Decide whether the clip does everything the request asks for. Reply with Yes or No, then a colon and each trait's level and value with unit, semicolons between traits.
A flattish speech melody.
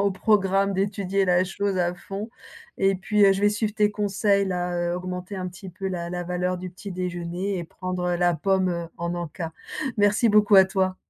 Yes: narrow, 2.0 semitones